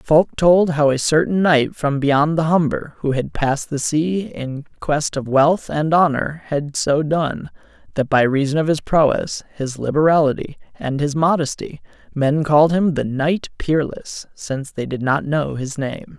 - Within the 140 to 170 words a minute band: No, average, 180 wpm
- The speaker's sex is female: No, male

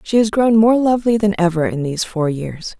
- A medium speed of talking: No, fast, 235 wpm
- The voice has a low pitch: No, high, 195 Hz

